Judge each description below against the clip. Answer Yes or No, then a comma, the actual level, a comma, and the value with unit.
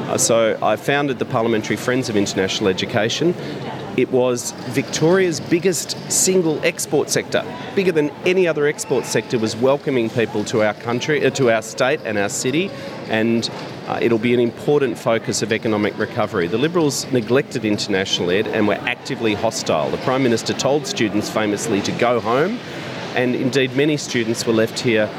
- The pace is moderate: Yes, average, 165 wpm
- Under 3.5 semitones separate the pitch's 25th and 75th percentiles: No, average, 4.6 semitones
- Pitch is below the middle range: Yes, low, 125 Hz